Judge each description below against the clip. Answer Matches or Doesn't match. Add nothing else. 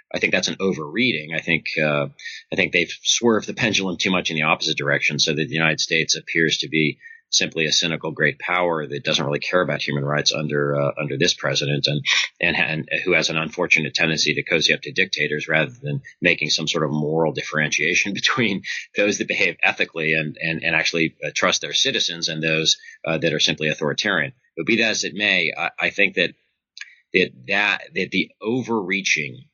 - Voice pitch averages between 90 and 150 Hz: Doesn't match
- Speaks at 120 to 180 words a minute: Doesn't match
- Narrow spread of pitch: Matches